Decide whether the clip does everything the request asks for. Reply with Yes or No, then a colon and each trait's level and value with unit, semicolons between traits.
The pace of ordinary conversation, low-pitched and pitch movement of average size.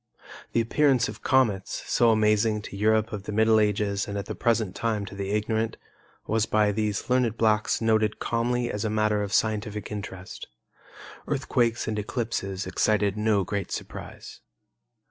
No: average, 160 wpm; low, 110 Hz; narrow, 1.7 semitones